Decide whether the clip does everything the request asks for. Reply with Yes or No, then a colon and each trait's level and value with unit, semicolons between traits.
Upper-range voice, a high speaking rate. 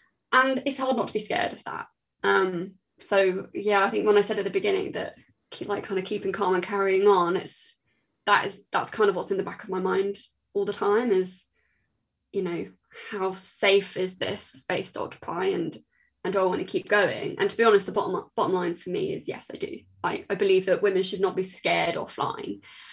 Yes: high, 200 Hz; fast, 235 wpm